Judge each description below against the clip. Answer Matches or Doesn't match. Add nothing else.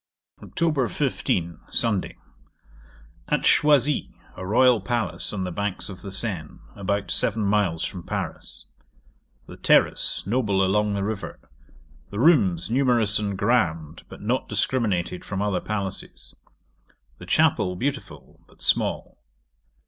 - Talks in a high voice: Doesn't match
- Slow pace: Matches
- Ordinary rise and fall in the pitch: Matches